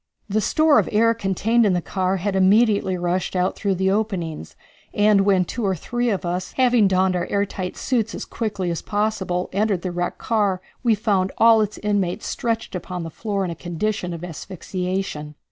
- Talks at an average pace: Yes, average, 195 wpm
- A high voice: Yes, high, 195 Hz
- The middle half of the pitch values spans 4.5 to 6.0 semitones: No, average, 3.0 semitones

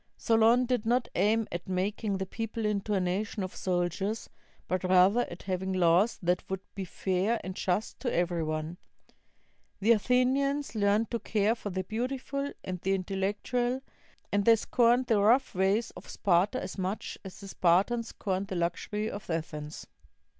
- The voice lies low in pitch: No, high, 200 Hz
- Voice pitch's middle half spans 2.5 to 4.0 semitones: Yes, average, 3.7 semitones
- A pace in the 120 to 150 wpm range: No, average, 165 wpm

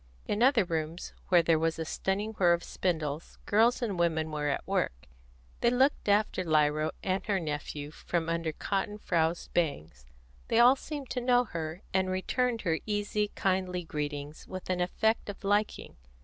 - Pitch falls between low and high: Yes, medium, 180 Hz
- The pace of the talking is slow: No, average, 170 wpm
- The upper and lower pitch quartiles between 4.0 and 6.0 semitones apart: Yes, average, 4.7 semitones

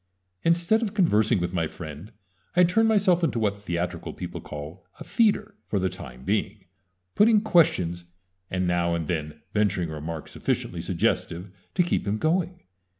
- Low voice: Yes, low, 100 Hz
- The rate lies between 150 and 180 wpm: Yes, average, 160 wpm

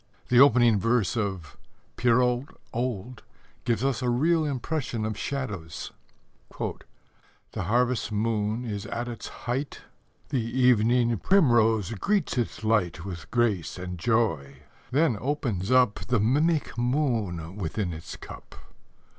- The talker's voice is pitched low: Yes, low, 115 Hz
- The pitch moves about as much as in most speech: Yes, average, 3.6 semitones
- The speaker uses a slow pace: Yes, slow, 120 wpm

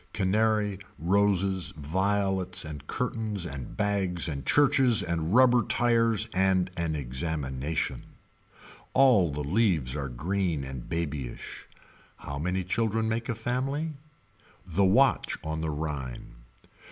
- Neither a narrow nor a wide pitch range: No, wide, 6.2 semitones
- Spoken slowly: Yes, slow, 115 wpm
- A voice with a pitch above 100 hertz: No, very low, 95 Hz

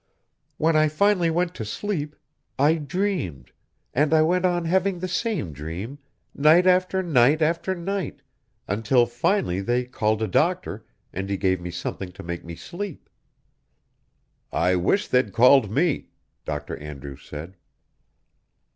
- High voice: No, medium, 145 Hz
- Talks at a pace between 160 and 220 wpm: No, average, 140 wpm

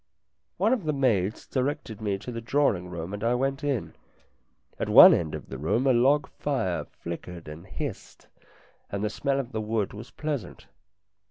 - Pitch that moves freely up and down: Yes, wide, 6.3 semitones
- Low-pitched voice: Yes, low, 115 Hz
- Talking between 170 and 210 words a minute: Yes, average, 180 wpm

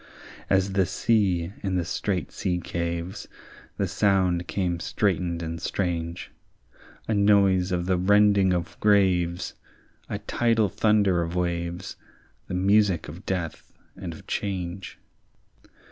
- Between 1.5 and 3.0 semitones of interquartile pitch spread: Yes, narrow, 2.4 semitones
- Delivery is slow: Yes, slow, 125 wpm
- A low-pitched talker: Yes, very low, 90 Hz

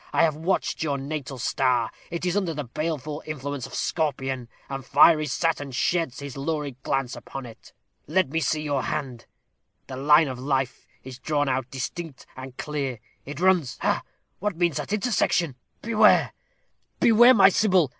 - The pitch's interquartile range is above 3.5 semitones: Yes, average, 3.9 semitones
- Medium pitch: Yes, medium, 145 Hz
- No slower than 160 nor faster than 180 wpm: Yes, average, 165 wpm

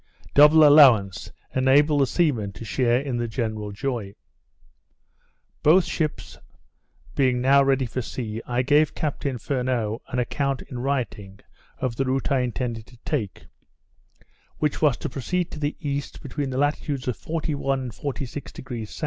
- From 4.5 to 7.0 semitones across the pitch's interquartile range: No, average, 3.2 semitones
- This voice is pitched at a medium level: No, low, 130 Hz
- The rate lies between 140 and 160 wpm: Yes, average, 150 wpm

